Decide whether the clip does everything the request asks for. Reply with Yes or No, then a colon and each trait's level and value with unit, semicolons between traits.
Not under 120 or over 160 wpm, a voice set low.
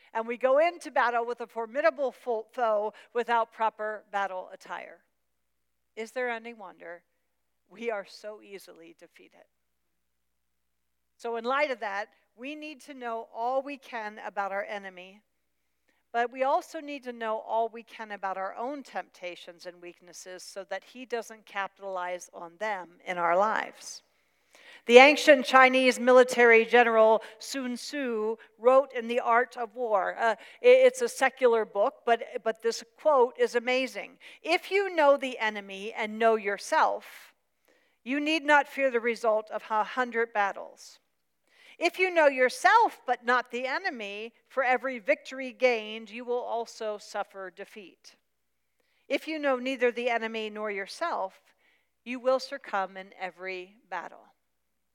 No: average, 145 wpm; high, 230 Hz